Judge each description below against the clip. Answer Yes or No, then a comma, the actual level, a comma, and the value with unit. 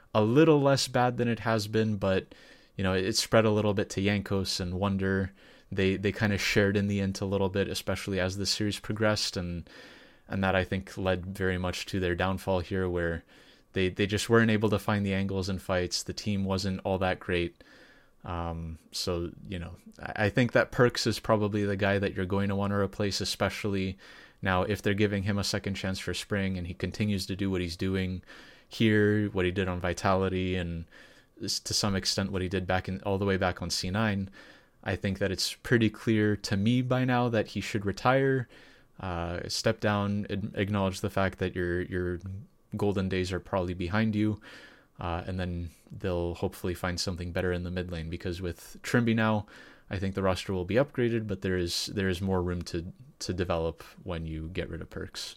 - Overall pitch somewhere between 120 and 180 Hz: No, very low, 95 Hz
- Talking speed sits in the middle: No, fast, 210 wpm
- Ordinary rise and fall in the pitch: No, narrow, 2.3 semitones